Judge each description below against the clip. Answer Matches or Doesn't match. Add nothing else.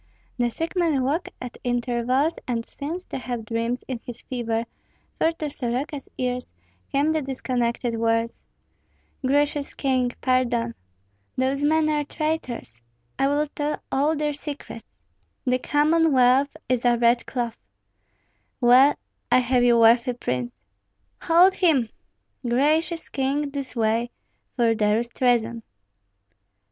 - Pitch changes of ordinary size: Matches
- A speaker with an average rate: Doesn't match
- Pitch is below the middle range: Doesn't match